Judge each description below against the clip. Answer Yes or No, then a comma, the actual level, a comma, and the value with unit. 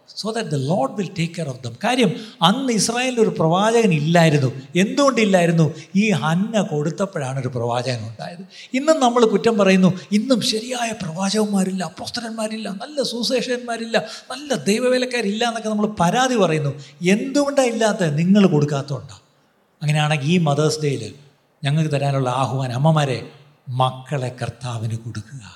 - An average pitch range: No, wide, 7.7 semitones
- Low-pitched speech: No, medium, 180 Hz